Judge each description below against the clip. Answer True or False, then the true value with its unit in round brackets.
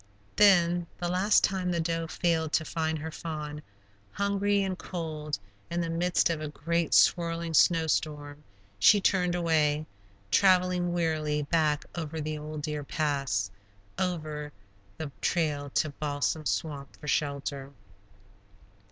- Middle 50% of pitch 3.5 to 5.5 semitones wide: False (2.6 semitones)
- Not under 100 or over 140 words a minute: True (135 wpm)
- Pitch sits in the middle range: True (160 Hz)